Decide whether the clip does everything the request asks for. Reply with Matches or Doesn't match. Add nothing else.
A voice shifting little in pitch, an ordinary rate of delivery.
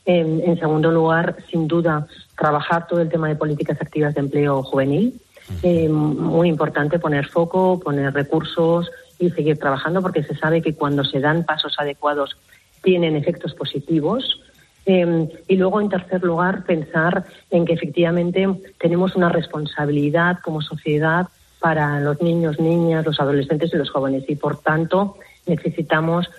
Matches